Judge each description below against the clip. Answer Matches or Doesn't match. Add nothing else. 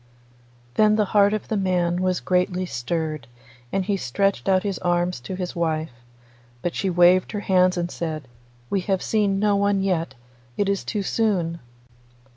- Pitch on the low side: Doesn't match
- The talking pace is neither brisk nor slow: Matches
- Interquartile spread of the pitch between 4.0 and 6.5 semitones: Doesn't match